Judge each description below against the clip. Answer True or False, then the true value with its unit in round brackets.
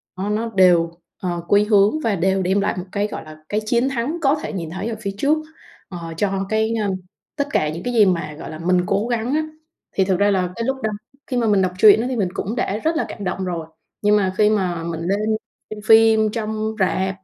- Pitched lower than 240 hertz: True (205 Hz)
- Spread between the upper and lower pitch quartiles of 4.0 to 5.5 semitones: False (3.3 semitones)